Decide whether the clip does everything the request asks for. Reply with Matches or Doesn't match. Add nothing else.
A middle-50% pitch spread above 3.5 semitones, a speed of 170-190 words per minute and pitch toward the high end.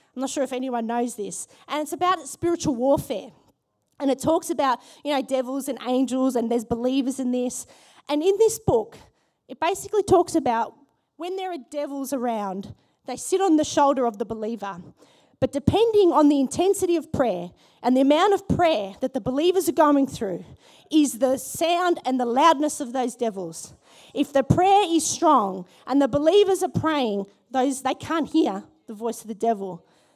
Matches